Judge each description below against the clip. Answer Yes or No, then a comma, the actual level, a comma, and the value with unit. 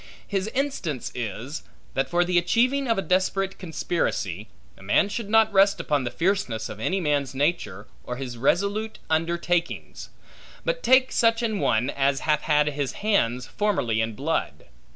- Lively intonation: Yes, wide, 7.3 semitones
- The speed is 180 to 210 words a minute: No, average, 160 wpm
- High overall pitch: No, medium, 170 Hz